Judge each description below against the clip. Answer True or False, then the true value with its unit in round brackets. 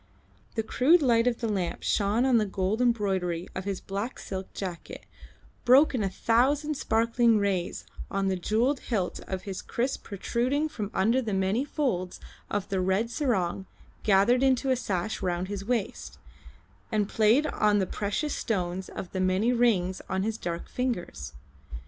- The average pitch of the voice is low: False (210 Hz)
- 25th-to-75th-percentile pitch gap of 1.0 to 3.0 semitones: False (4.3 semitones)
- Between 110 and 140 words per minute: False (165 wpm)